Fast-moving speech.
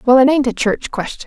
Yes: fast, 285 wpm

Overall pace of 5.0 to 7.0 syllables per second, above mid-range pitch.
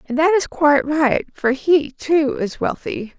No: 4.0 syllables/s; very high, 295 Hz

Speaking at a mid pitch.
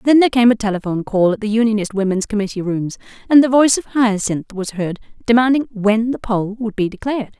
No: high, 220 Hz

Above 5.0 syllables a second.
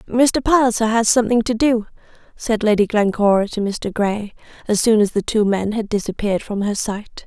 Yes: 5.3 syllables/s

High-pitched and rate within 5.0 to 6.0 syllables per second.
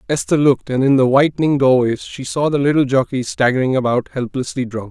No: low, 130 Hz; 5.9 syllables/s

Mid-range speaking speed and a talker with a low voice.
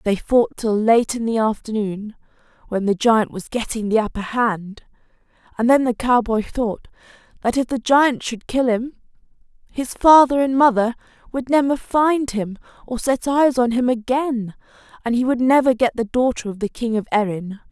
No: average, 180 wpm; high, 240 Hz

